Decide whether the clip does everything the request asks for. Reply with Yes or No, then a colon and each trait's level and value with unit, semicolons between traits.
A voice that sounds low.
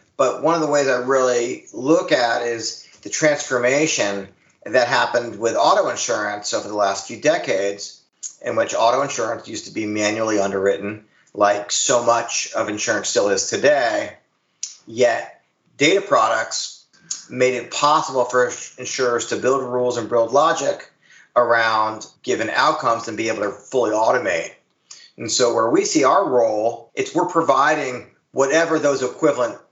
Yes: low, 125 Hz